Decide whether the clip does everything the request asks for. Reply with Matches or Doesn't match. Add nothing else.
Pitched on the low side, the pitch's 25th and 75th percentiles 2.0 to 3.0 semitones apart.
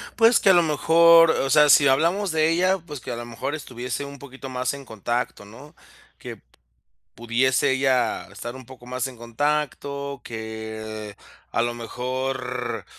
Doesn't match